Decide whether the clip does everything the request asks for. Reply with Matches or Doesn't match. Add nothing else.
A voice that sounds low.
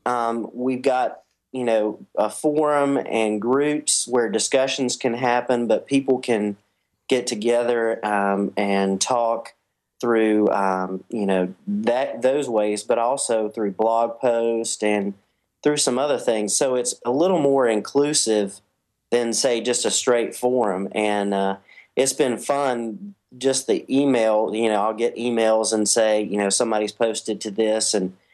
Matches